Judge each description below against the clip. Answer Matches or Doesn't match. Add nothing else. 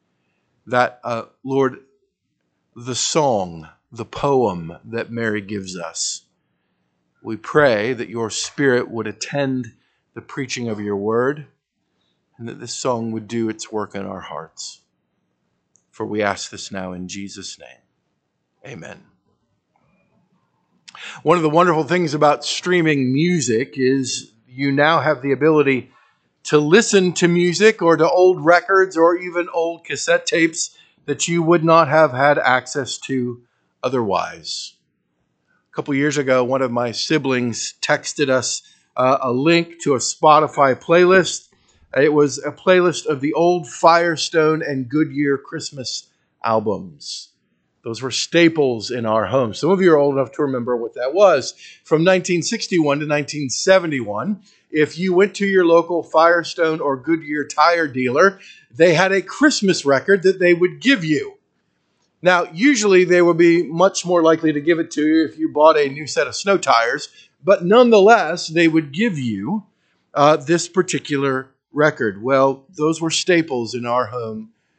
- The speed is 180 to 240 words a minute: Doesn't match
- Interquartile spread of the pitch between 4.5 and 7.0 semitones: Matches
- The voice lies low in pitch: Doesn't match